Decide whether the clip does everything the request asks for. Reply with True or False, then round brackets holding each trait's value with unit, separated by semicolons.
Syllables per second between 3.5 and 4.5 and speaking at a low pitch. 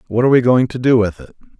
False (7.1 syllables/s; 120 Hz)